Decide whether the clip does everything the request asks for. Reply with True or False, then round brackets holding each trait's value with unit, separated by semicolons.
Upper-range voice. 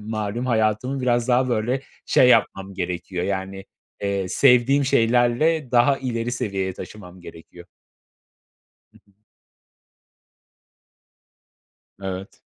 False (115 Hz)